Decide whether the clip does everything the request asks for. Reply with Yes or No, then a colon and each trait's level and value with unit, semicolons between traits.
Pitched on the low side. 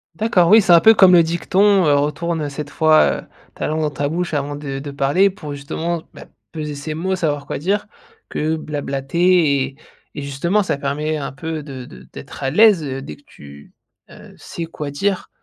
No: medium, 155 Hz